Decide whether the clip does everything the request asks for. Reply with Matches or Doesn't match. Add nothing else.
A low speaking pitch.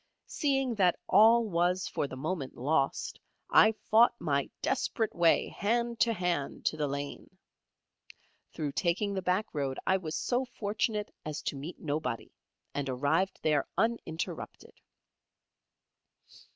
Doesn't match